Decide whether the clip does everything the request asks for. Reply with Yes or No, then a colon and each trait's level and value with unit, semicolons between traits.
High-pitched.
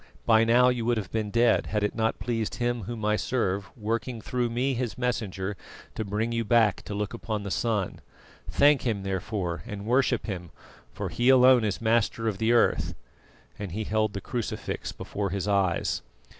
No: low, 110 Hz